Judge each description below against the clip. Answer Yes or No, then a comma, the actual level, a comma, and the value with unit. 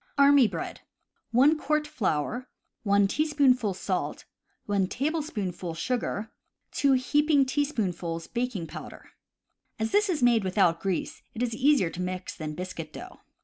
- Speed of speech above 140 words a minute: No, slow, 135 wpm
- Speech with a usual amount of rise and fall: No, wide, 7.3 semitones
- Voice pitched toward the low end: No, high, 225 Hz